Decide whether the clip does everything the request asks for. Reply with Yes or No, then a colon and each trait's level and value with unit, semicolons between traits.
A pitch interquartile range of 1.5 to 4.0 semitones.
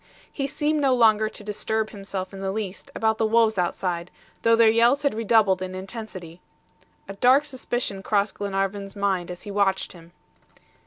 Yes: average, 3.0 semitones